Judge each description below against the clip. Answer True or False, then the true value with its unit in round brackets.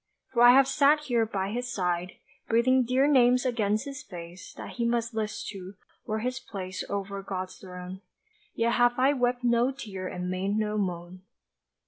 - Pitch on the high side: True (225 Hz)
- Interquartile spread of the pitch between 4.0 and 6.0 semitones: True (4.7 semitones)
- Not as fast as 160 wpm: False (175 wpm)